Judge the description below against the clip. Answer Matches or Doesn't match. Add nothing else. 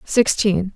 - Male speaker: Doesn't match